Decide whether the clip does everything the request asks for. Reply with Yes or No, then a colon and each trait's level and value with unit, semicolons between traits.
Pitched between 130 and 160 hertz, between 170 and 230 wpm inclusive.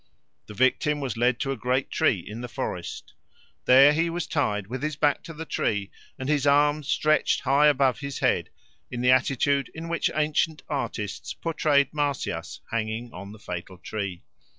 Yes: low, 135 Hz; average, 175 wpm